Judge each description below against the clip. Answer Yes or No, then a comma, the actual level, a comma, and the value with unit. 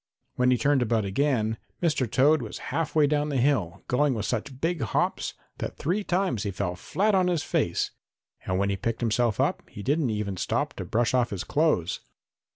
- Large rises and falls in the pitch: Yes, wide, 5.9 semitones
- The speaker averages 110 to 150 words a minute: No, average, 200 wpm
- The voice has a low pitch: Yes, low, 125 Hz